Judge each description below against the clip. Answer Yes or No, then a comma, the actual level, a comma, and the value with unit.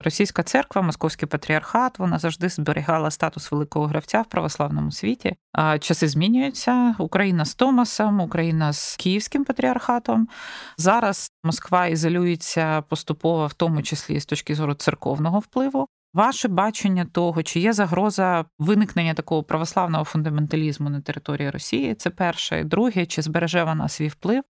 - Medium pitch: Yes, medium, 170 Hz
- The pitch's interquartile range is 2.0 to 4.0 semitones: No, average, 4.8 semitones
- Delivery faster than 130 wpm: Yes, average, 140 wpm